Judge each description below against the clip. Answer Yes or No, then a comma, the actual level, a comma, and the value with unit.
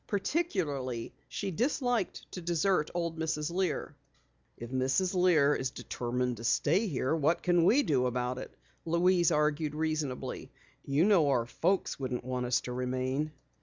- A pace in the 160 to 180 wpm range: No, average, 150 wpm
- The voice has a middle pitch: Yes, medium, 150 Hz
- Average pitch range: No, wide, 5.7 semitones